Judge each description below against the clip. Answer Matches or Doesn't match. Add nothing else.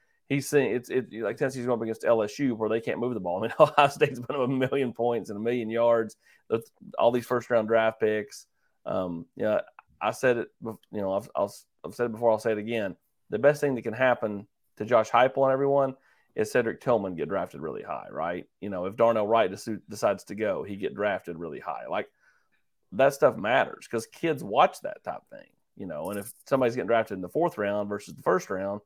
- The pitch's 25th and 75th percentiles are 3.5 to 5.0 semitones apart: Doesn't match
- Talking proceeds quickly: Matches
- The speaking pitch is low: Matches